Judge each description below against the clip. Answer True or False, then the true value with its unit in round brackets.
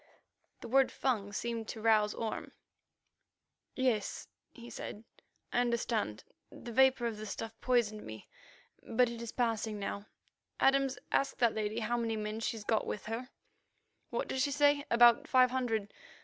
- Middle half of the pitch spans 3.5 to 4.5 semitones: False (2.6 semitones)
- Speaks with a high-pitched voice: True (230 Hz)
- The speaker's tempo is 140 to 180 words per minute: True (155 wpm)